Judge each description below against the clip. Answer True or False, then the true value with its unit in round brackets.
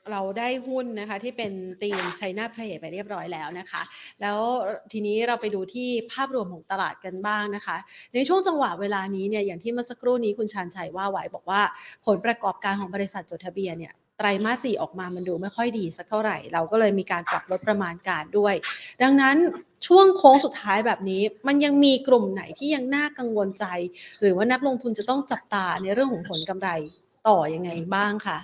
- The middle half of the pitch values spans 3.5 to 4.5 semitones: True (4.1 semitones)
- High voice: True (205 Hz)